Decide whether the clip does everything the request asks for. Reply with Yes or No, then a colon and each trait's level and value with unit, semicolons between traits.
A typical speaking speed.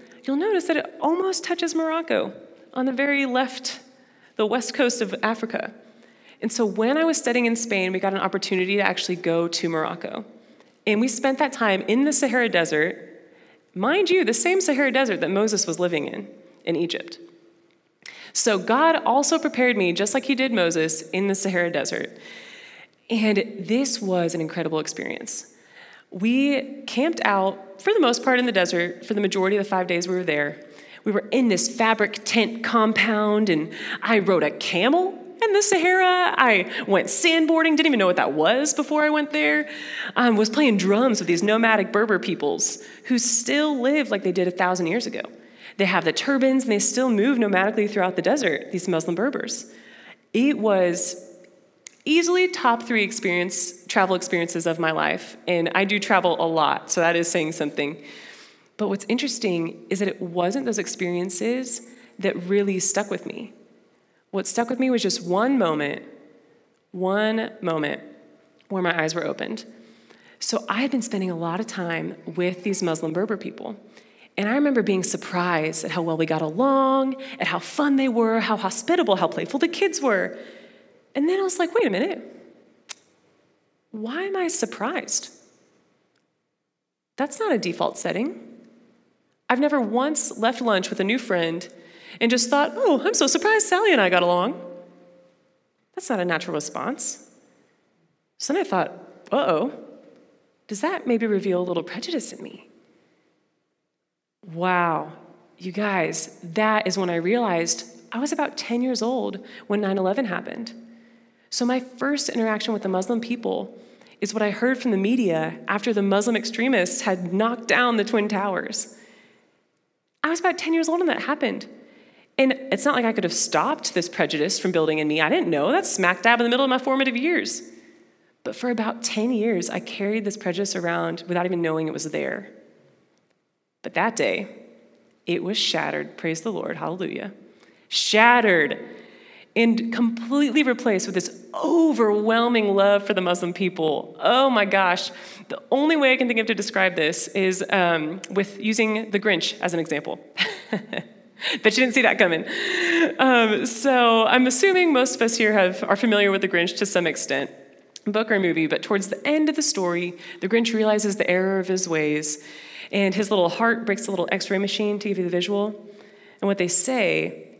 Yes: average, 180 wpm